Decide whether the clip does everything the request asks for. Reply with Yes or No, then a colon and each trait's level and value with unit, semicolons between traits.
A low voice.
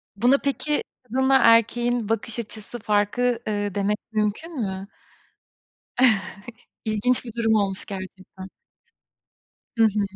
No: high, 220 Hz